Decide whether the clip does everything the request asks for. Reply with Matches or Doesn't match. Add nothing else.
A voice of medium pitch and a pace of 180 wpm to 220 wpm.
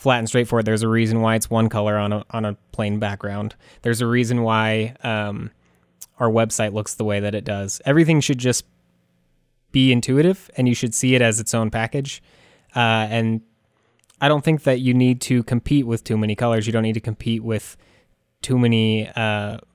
Doesn't match